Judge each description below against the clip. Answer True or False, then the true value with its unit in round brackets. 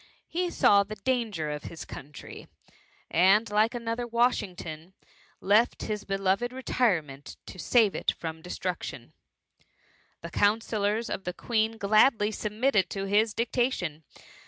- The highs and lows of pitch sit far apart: False (4.0 semitones)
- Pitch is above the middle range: True (210 Hz)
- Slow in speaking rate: True (130 wpm)